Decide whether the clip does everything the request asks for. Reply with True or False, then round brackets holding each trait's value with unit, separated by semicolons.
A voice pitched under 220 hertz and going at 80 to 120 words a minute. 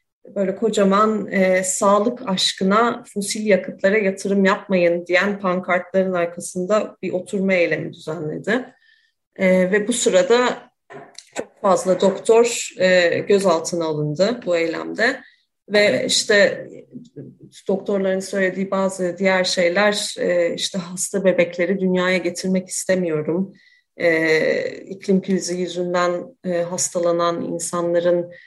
True (190 Hz; 105 wpm)